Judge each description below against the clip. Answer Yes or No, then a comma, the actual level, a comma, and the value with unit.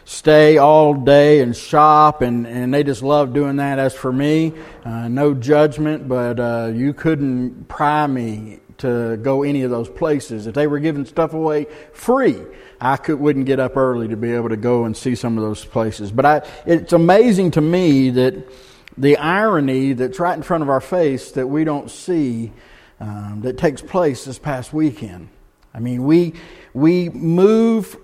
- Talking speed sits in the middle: Yes, average, 195 wpm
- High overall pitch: No, medium, 140 Hz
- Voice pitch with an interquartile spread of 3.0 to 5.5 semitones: Yes, average, 3.8 semitones